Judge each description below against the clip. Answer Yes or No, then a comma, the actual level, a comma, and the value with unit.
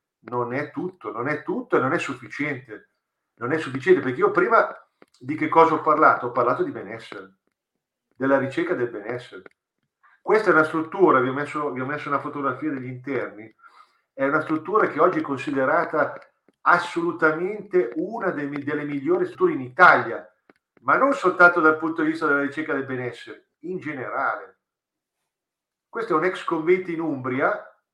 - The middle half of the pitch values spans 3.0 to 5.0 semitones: Yes, average, 3.9 semitones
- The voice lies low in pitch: No, medium, 155 Hz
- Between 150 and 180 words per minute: Yes, average, 165 wpm